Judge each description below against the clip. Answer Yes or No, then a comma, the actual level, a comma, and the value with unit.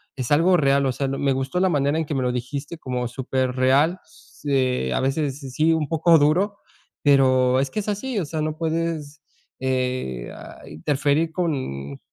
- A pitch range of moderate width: Yes, average, 3.7 semitones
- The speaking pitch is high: No, medium, 140 Hz